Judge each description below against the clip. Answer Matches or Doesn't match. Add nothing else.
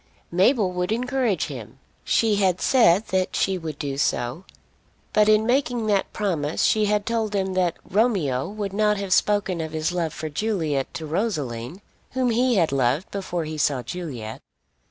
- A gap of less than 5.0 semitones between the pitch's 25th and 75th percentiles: Doesn't match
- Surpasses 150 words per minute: Matches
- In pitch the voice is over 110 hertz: Matches